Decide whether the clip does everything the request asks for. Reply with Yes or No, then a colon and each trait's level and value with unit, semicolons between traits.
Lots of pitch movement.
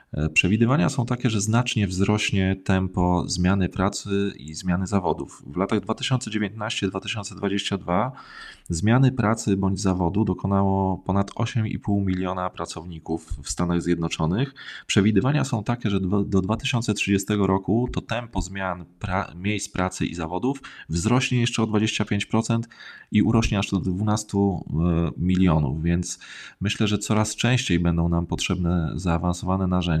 No: average, 3.1 semitones